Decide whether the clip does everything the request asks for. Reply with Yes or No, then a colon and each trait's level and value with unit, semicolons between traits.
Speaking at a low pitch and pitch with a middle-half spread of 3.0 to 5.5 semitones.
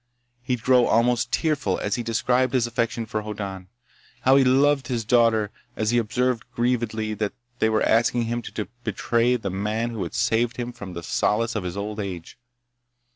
No: low, 115 Hz; narrow, 2.5 semitones